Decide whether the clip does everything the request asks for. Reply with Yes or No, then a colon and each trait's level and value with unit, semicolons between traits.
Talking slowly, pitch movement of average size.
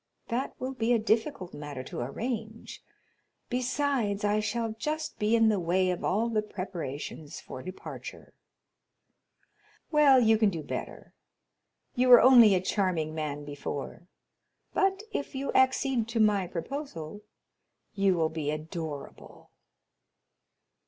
No: slow, 130 wpm; wide, 6.7 semitones